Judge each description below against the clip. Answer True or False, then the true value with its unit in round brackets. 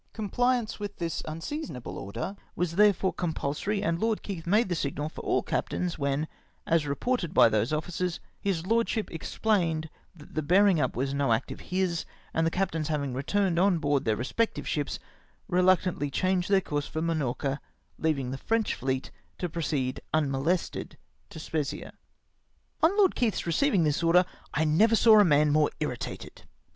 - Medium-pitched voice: True (165 Hz)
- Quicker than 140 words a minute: True (170 wpm)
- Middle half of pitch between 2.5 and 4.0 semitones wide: False (5.0 semitones)